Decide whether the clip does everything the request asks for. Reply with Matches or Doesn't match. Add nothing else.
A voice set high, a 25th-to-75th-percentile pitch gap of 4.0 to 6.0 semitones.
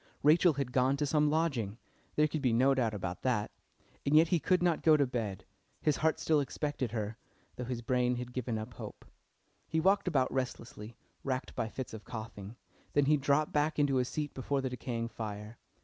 Doesn't match